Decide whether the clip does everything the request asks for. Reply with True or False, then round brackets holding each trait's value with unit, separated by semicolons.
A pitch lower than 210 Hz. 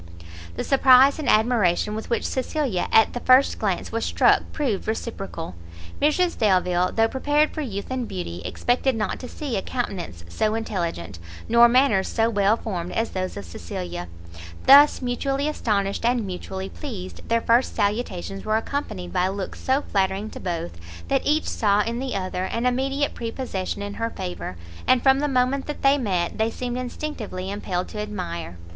False (220 Hz)